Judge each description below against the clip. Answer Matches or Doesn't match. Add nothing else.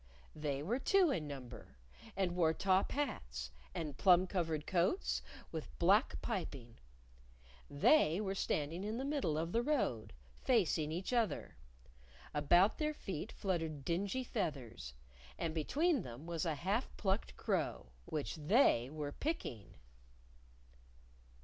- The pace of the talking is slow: Matches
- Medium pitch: Matches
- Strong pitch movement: Matches